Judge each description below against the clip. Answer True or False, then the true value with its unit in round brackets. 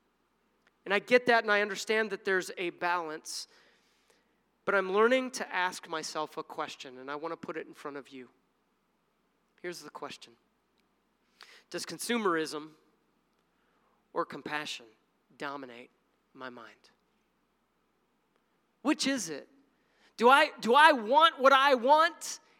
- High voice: True (205 Hz)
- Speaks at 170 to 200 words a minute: False (135 wpm)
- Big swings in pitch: True (7.5 semitones)